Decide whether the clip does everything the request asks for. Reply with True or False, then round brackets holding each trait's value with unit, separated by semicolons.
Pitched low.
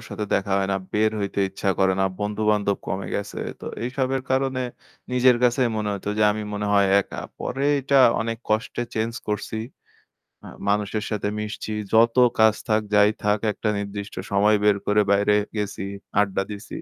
True (105 Hz)